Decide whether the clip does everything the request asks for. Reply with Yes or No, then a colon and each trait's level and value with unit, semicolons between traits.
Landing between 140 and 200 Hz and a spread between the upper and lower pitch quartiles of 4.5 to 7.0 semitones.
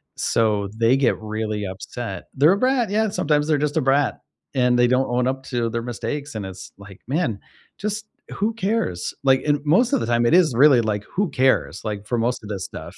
No: low, 125 Hz; wide, 5.6 semitones